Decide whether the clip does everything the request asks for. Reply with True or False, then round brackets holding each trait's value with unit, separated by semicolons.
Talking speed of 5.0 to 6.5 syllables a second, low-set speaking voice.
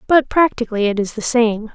False (5.7 syllables/s; 235 Hz)